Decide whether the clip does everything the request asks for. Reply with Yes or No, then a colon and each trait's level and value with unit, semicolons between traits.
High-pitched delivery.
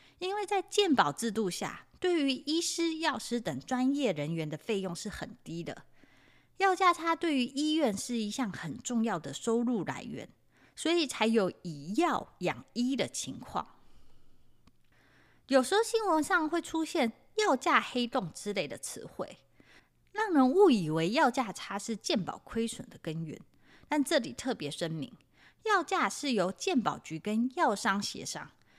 Yes: very high, 250 Hz